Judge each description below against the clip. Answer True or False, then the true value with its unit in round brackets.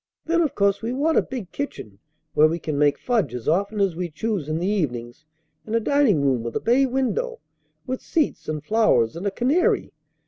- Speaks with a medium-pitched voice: False (200 Hz)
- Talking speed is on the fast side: True (210 wpm)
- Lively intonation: True (9.0 semitones)